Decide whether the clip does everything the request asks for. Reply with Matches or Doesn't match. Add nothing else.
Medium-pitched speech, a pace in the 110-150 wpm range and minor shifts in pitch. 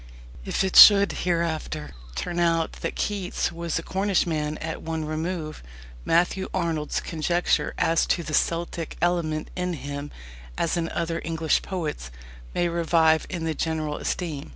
Matches